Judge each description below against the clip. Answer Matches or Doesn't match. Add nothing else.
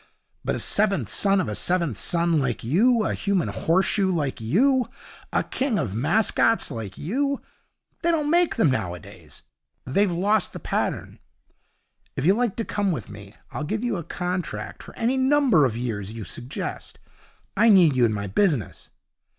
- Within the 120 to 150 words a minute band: Doesn't match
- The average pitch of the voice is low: Doesn't match